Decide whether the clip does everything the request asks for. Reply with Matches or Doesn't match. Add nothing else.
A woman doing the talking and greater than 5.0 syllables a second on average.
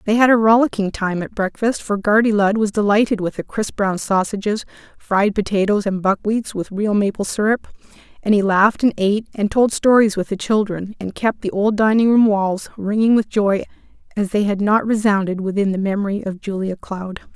Matches